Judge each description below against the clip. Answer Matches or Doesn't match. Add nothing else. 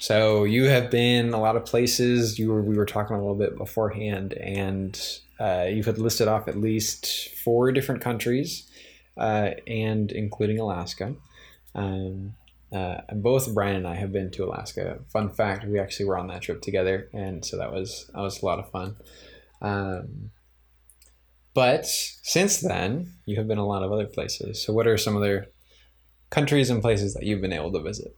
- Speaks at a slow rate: Doesn't match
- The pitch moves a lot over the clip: Doesn't match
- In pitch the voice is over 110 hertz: Doesn't match